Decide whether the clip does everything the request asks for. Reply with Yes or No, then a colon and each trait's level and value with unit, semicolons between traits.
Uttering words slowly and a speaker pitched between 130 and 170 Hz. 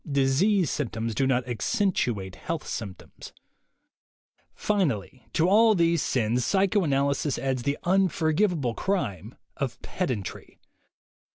Yes: slow, 100 wpm; medium, 140 Hz